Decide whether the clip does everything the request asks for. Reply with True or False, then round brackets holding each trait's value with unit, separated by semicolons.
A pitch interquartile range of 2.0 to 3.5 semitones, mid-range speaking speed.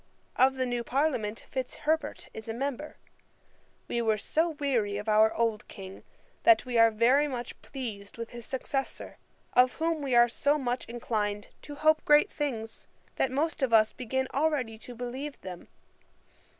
False (4.2 semitones; 160 wpm)